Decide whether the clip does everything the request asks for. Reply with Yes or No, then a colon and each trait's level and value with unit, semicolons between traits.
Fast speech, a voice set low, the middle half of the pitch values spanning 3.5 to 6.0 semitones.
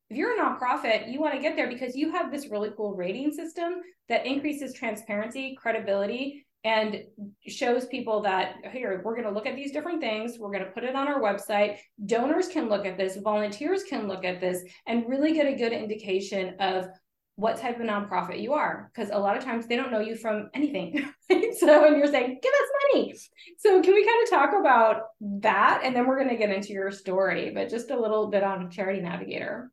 No: fast, 220 wpm; high, 230 Hz; wide, 5.5 semitones